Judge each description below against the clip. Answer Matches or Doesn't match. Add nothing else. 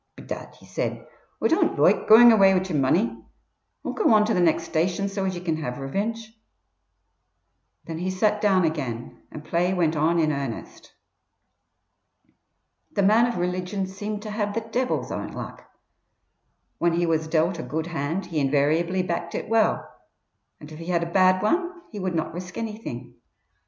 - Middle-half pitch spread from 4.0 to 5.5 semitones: Matches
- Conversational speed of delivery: Matches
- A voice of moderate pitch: Matches